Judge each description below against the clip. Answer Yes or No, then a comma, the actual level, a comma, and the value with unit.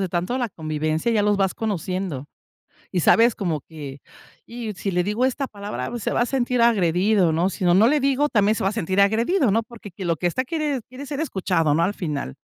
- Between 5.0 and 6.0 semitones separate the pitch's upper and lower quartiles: Yes, average, 5.3 semitones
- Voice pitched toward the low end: No, high, 200 Hz